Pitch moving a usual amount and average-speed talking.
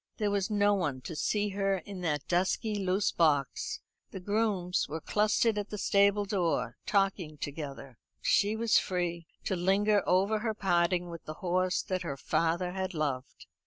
Yes: average, 3.4 semitones; average, 165 wpm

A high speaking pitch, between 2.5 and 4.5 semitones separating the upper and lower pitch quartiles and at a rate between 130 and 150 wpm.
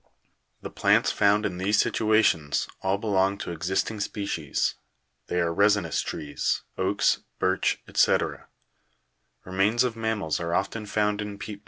No: low, 100 Hz; average, 3.0 semitones; slow, 135 wpm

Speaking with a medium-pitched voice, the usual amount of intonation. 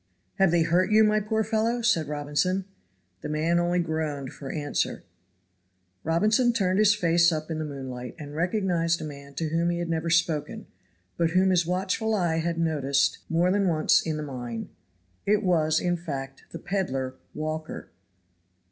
Yes: medium, 165 Hz; average, 3.4 semitones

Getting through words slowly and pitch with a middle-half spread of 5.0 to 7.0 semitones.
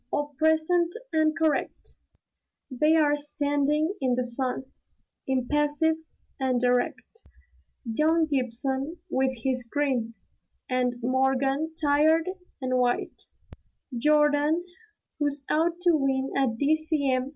No: slow, 100 wpm; average, 3.3 semitones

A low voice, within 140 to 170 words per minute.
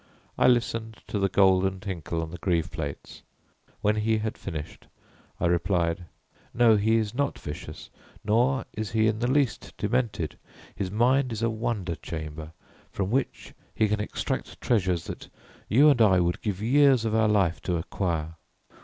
Yes: low, 105 Hz; average, 165 wpm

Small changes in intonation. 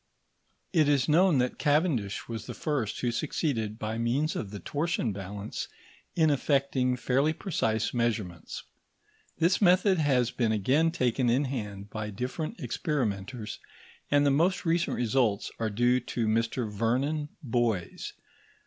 No: average, 5.1 semitones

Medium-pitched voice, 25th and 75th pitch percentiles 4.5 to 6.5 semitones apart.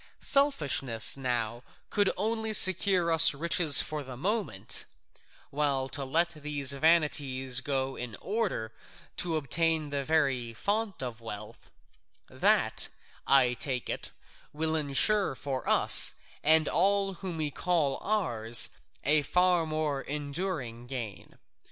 Yes: medium, 150 Hz; average, 4.8 semitones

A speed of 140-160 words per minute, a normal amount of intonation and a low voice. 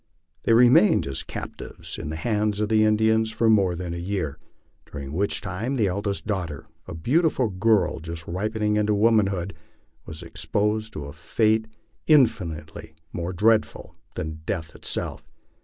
Yes: average, 150 wpm; average, 4.7 semitones; low, 100 Hz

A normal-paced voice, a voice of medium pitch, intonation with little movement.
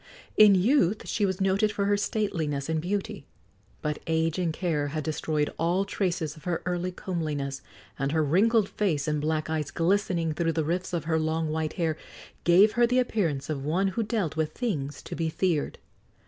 No: average, 190 wpm; medium, 165 Hz; average, 3.9 semitones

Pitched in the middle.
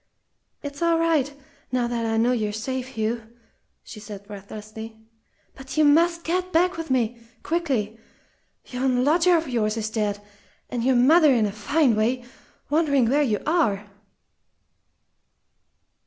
No: very high, 250 Hz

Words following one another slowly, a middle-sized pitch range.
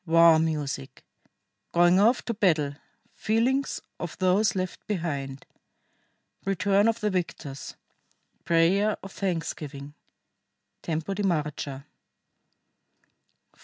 Yes: slow, 95 wpm; average, 4.6 semitones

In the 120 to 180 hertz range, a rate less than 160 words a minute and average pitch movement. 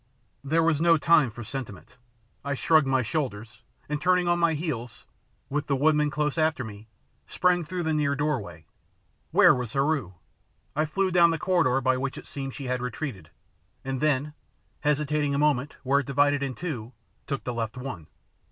No: medium, 140 Hz; average, 180 wpm; average, 3.6 semitones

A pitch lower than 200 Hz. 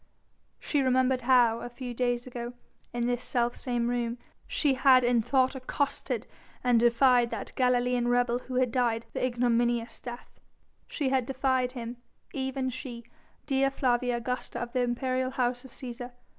No: high, 245 Hz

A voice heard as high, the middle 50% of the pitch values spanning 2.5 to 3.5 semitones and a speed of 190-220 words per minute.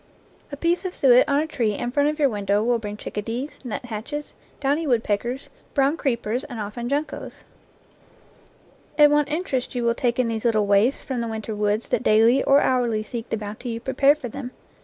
No: high, 245 Hz; average, 4.2 semitones; average, 200 wpm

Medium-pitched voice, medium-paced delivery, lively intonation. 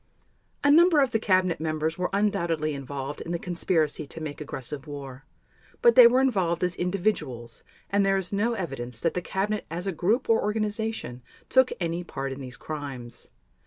Yes: medium, 175 Hz; average, 180 wpm; wide, 6.2 semitones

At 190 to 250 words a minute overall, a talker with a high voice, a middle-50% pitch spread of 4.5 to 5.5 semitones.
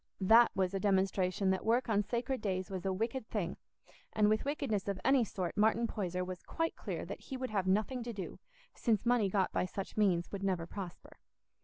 No: fast, 205 wpm; high, 200 Hz; average, 3.6 semitones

